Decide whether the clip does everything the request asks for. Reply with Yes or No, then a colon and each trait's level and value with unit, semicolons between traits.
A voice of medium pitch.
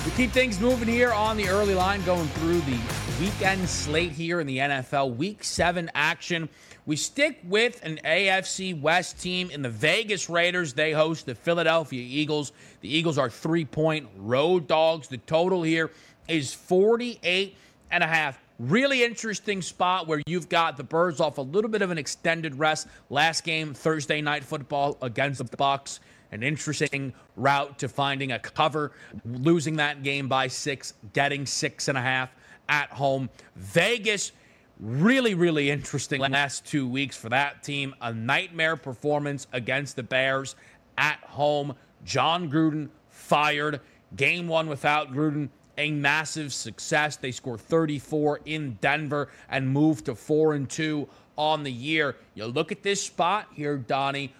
Yes: medium, 150 Hz